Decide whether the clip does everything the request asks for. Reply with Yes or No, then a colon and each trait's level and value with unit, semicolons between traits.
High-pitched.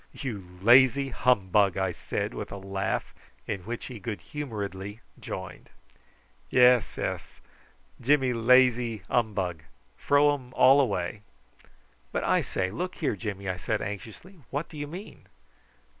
No: low, 115 Hz